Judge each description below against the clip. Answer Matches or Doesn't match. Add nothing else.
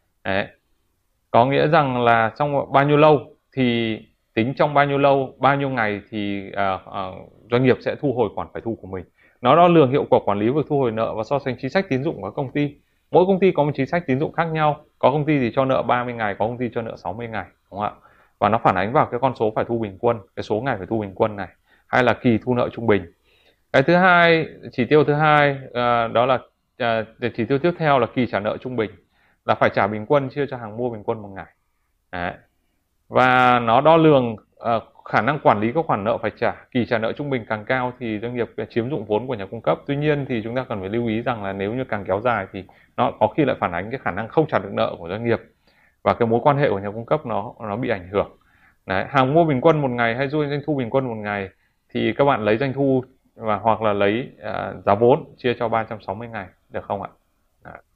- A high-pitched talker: Doesn't match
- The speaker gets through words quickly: Matches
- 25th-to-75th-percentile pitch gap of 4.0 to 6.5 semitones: Matches